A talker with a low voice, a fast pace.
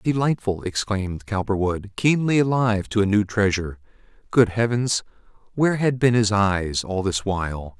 No: low, 105 Hz; average, 145 wpm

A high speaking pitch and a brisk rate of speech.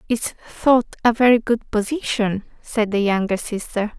No: high, 225 Hz; average, 150 wpm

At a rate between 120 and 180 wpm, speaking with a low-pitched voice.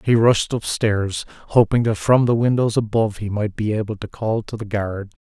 No: fast, 205 wpm; low, 110 Hz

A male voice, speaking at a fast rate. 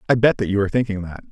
Yes: male; fast, 320 wpm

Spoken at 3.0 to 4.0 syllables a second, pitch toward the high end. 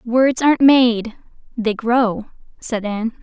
Yes: 3.6 syllables/s; high, 235 Hz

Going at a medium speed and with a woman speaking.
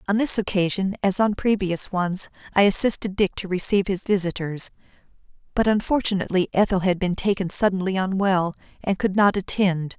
Yes: average, 155 wpm; female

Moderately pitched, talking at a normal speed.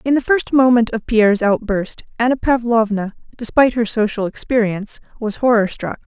No: high, 225 Hz; average, 155 wpm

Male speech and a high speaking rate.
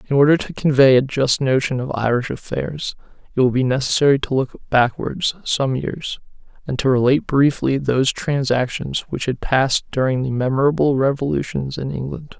No: male; average, 165 wpm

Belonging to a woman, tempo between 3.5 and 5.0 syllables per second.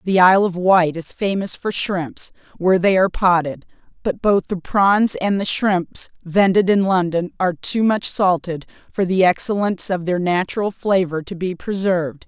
Yes: female; 4.8 syllables/s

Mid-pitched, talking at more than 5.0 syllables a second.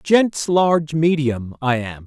No: medium, 150 Hz; 3.5 syllables/s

